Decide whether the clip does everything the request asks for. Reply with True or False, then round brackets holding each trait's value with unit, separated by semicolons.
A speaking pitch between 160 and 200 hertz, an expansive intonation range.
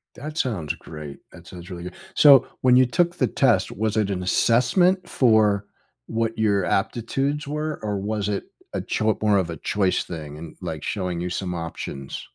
False (105 Hz; 5.8 semitones)